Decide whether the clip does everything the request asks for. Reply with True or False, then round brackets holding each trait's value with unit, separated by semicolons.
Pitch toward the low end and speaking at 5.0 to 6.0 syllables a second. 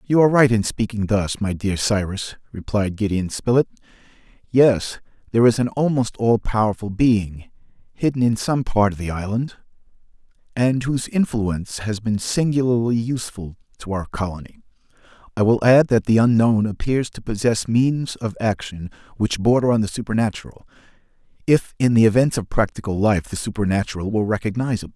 True (110 Hz; 5.4 syllables/s)